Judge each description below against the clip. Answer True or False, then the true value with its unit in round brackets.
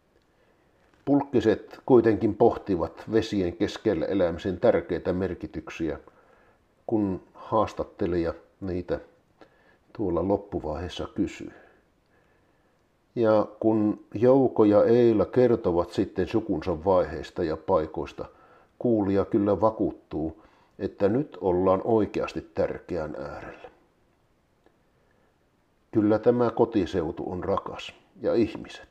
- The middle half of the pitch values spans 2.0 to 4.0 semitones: True (3.3 semitones)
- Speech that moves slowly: True (85 wpm)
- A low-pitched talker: True (110 Hz)